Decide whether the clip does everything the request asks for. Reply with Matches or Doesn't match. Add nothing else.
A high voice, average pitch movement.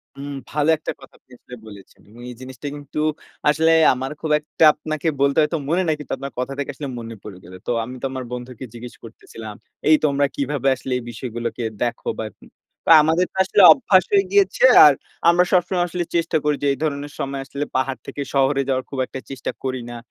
Doesn't match